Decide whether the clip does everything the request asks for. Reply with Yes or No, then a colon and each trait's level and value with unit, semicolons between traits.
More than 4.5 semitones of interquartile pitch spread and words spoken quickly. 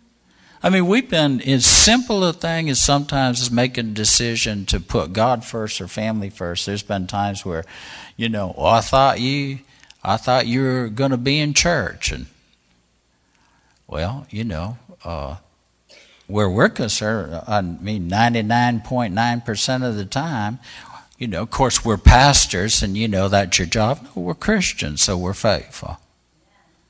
No: average, 5.1 semitones; average, 165 wpm